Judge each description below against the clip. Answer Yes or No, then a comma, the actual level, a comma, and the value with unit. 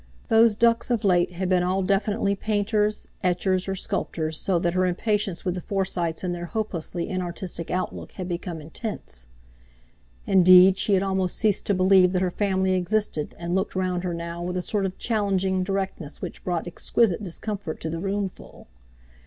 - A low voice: No, medium, 185 Hz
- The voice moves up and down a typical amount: No, narrow, 2.2 semitones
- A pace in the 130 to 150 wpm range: No, average, 175 wpm